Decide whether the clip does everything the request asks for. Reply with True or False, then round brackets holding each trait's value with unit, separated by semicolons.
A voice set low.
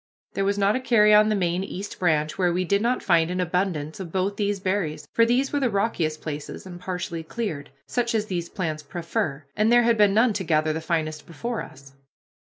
False (185 Hz)